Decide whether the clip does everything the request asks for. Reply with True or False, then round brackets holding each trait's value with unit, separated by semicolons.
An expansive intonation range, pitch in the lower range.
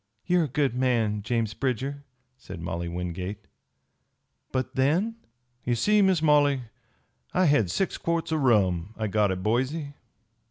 True (6.1 semitones; 125 Hz)